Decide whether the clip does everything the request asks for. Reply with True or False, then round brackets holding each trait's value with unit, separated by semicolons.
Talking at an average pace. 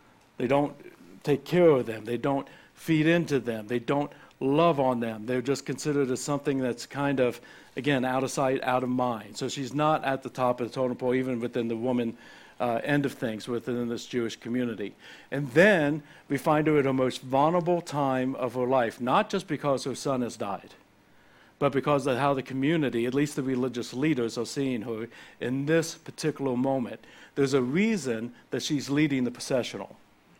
True (195 wpm)